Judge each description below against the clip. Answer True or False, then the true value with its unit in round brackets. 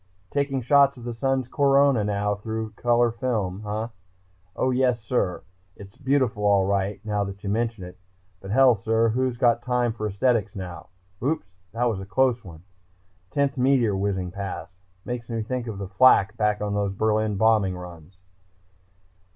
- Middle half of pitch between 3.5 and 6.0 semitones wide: True (3.9 semitones)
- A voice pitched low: True (110 Hz)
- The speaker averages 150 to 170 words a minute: True (165 wpm)